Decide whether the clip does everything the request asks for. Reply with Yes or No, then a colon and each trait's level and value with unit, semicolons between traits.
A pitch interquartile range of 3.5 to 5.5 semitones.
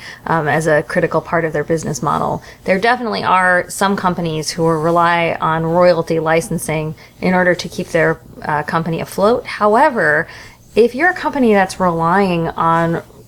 No: average, 2.7 semitones